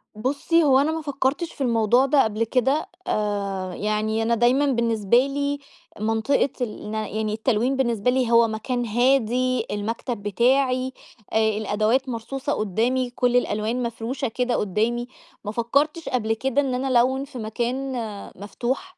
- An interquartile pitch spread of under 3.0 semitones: No, average, 3.3 semitones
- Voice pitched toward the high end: Yes, high, 240 Hz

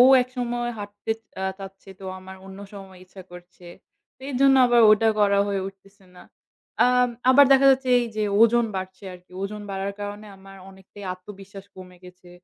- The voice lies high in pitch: Yes, high, 195 Hz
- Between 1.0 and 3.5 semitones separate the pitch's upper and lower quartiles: Yes, average, 2.9 semitones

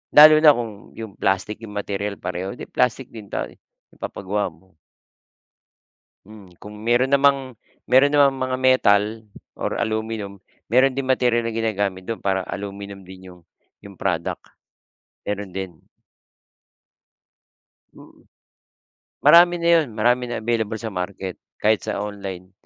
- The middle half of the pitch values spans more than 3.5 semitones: Yes, average, 4.3 semitones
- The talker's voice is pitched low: Yes, low, 105 Hz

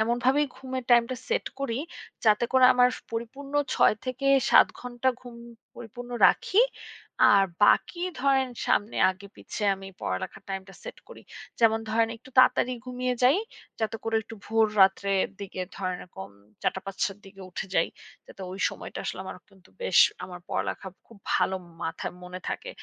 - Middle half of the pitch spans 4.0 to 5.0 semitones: Yes, average, 4.6 semitones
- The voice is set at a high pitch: Yes, high, 225 Hz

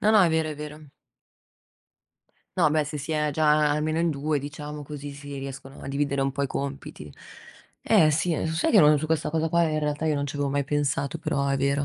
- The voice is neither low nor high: Yes, medium, 150 Hz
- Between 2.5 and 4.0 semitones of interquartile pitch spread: No, narrow, 1.8 semitones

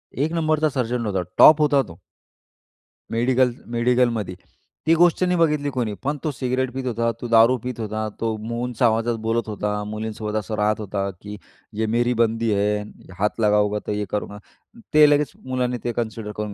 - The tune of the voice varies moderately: Yes, average, 3.5 semitones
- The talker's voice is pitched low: Yes, low, 115 Hz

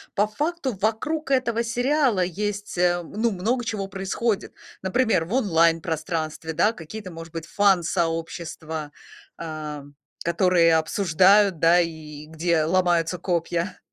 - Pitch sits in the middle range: Yes, medium, 180 Hz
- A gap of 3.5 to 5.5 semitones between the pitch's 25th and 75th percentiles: Yes, average, 4.4 semitones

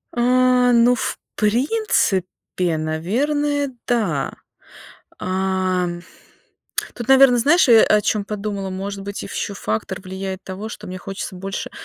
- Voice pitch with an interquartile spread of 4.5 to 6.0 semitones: Yes, average, 4.8 semitones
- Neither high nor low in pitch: No, high, 200 Hz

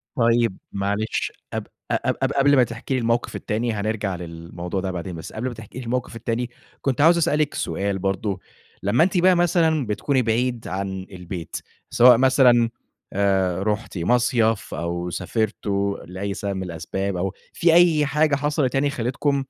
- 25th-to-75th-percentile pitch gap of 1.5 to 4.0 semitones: No, average, 5.3 semitones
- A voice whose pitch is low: Yes, low, 115 Hz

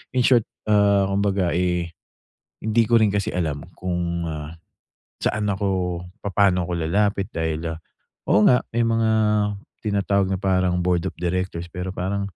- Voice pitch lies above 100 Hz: No, very low, 95 Hz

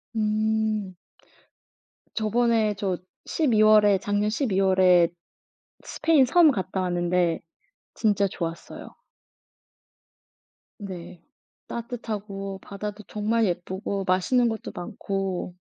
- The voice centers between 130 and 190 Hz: No, high, 205 Hz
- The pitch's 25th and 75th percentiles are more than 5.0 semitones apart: No, average, 2.7 semitones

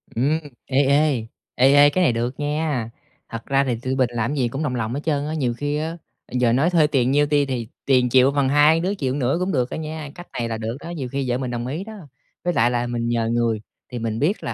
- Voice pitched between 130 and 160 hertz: Yes, low, 135 Hz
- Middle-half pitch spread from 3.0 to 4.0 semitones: Yes, average, 3.7 semitones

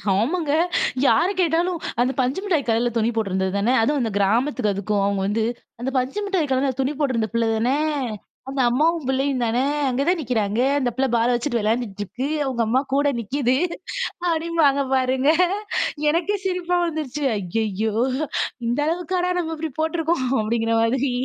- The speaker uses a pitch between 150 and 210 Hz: No, very high, 260 Hz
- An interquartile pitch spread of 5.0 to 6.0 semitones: Yes, wide, 5.5 semitones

